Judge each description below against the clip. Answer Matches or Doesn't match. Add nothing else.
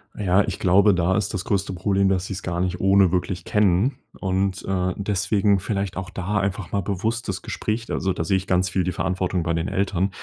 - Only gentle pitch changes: Matches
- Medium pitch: Doesn't match